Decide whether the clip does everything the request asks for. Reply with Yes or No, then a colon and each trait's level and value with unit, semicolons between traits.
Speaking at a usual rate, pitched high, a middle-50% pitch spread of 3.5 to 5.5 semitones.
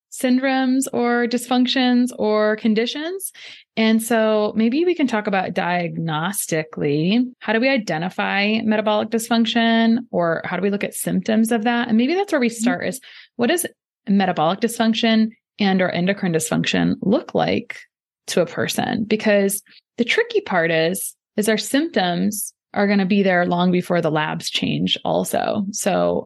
Yes: average, 155 wpm; high, 215 Hz; average, 4.5 semitones